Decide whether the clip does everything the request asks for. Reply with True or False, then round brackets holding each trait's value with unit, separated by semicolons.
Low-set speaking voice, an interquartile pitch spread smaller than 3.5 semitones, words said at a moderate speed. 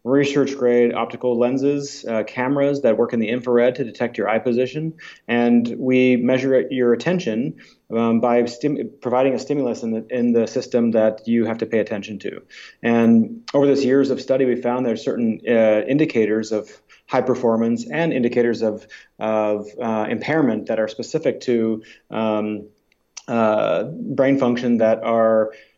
True (120 Hz; 2.7 semitones; 160 wpm)